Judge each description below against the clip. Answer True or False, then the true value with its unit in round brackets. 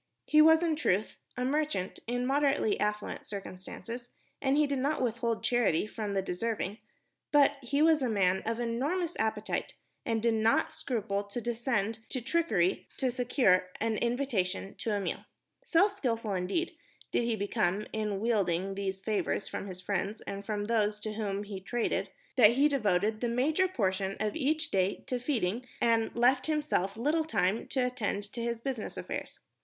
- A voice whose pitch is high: True (230 Hz)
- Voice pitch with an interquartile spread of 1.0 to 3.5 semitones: False (4.6 semitones)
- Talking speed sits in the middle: True (170 wpm)